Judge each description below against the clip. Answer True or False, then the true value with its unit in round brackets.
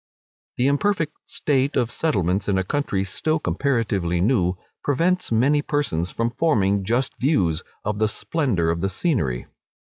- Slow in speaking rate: False (145 wpm)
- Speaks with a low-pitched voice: True (115 Hz)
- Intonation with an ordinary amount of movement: False (7.4 semitones)